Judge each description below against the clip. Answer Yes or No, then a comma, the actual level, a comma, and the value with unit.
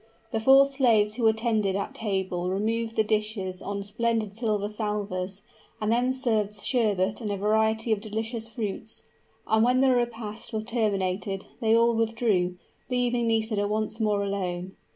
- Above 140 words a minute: Yes, average, 150 wpm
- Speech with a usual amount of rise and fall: No, narrow, 2.2 semitones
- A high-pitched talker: Yes, high, 220 Hz